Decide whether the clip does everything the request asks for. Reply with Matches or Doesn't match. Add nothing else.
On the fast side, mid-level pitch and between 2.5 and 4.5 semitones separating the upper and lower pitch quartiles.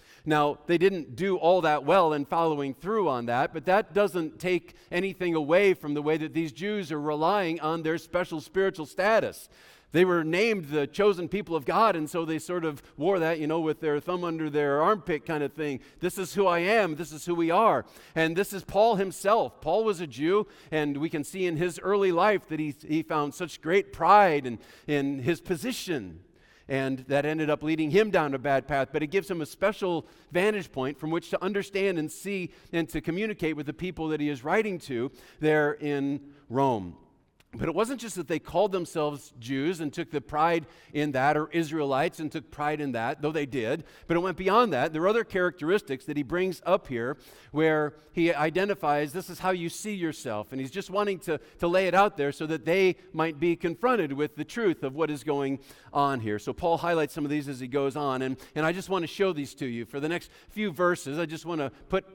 Matches